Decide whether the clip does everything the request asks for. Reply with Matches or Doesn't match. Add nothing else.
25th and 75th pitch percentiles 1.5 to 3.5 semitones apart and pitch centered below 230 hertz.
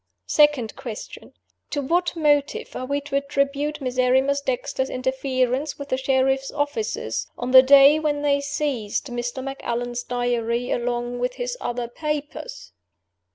Doesn't match